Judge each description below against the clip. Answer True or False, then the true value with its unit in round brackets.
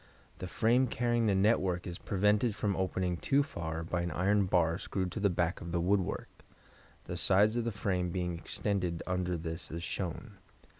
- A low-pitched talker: True (95 Hz)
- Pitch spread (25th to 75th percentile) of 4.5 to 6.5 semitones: False (3.1 semitones)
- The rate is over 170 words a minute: True (185 wpm)